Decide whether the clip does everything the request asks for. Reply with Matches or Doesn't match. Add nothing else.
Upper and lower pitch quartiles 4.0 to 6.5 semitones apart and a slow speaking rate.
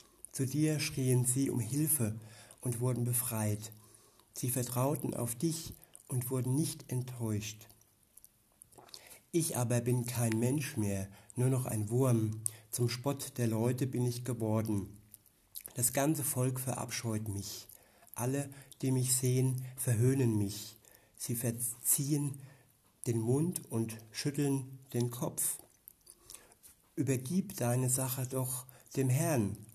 Doesn't match